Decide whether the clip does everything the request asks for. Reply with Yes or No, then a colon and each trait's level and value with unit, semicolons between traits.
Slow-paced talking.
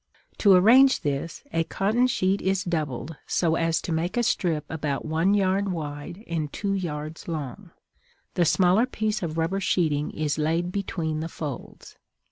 No: average, 160 wpm